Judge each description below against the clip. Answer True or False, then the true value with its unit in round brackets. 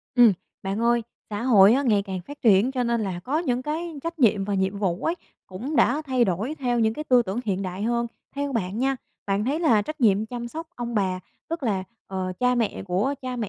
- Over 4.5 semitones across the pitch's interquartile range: True (4.9 semitones)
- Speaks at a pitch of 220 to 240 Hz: True (235 Hz)